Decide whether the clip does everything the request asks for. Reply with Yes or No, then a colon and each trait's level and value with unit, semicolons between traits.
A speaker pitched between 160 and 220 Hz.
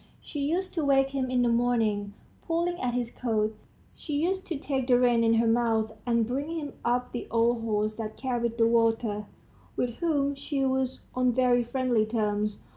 No: high, 245 Hz